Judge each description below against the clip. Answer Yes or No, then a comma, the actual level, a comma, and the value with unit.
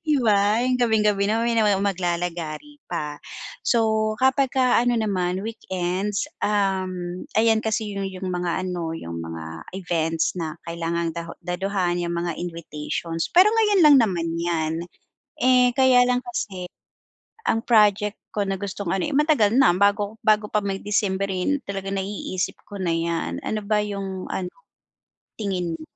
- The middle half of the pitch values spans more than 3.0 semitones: Yes, average, 4.0 semitones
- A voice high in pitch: Yes, high, 195 Hz